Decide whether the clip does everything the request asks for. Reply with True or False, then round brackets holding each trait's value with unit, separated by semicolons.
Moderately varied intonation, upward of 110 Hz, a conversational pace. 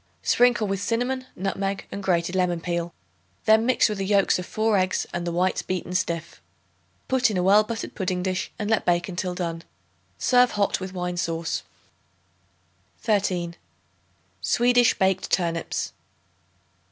True (3.3 semitones; 190 Hz; 150 wpm)